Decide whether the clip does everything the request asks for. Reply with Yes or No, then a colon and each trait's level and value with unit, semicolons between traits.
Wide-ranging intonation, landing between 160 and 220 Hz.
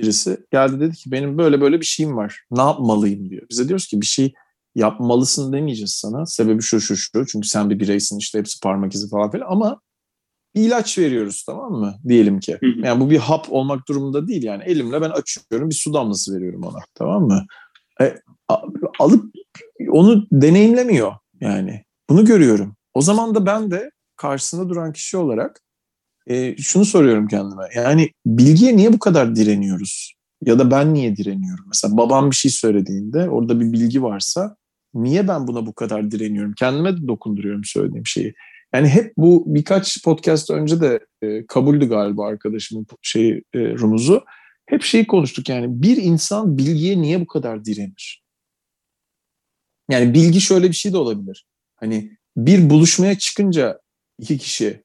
No: wide, 8.5 semitones; low, 135 Hz